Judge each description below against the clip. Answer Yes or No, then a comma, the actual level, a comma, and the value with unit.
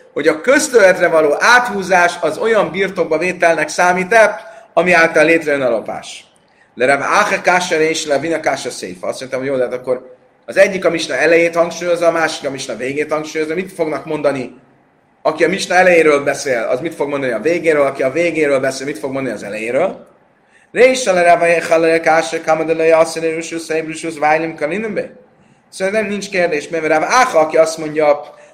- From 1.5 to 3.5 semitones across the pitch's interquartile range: Yes, average, 2.8 semitones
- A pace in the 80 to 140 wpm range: No, average, 150 wpm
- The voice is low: No, medium, 165 Hz